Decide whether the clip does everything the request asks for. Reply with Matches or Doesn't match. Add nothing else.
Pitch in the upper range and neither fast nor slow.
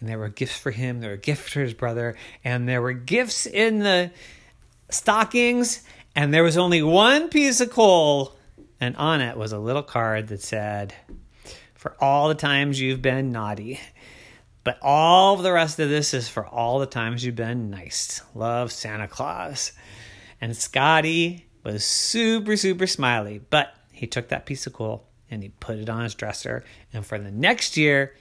Doesn't match